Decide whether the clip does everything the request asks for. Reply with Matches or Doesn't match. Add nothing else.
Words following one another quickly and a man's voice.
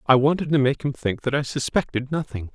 Matches